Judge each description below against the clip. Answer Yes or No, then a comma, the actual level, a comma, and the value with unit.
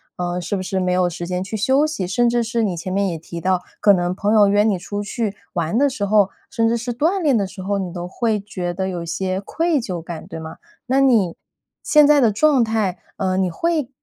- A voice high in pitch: Yes, high, 200 Hz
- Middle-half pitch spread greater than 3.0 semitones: Yes, average, 4.5 semitones